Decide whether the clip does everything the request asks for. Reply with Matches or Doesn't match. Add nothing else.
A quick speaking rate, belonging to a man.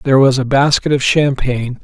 Doesn't match